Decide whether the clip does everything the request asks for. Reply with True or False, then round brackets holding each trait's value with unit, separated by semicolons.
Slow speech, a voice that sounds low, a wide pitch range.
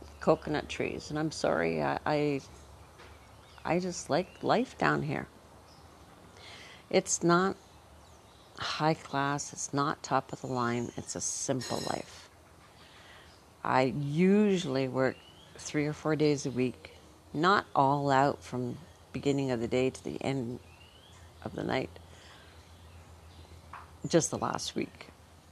True (125 wpm; 120 Hz; 8.6 semitones)